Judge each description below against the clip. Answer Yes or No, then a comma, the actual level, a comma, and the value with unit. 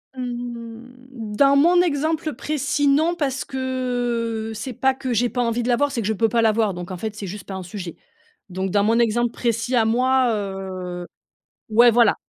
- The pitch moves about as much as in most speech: Yes, average, 3.4 semitones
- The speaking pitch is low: No, high, 235 Hz